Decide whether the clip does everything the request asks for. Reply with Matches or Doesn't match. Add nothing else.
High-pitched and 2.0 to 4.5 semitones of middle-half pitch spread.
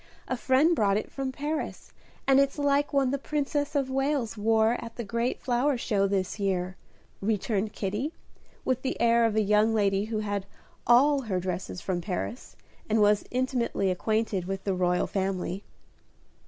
Doesn't match